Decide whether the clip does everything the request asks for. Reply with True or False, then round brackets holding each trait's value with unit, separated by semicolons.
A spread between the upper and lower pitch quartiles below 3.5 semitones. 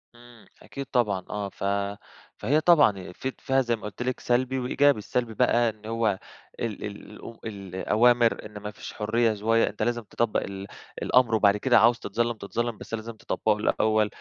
True (2.4 semitones)